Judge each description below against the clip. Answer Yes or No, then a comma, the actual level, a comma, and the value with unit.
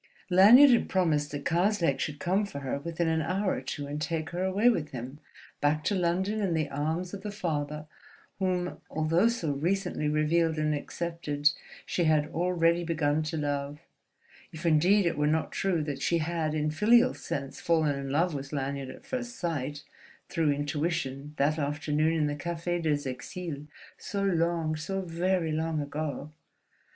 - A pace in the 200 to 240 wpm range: No, average, 170 wpm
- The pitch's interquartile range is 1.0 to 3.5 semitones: Yes, average, 3.1 semitones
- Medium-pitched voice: Yes, medium, 160 Hz